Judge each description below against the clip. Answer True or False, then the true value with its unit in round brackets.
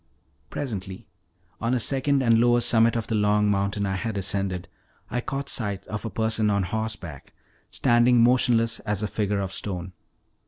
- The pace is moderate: True (165 wpm)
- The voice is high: False (110 Hz)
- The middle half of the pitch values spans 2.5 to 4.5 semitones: True (3.1 semitones)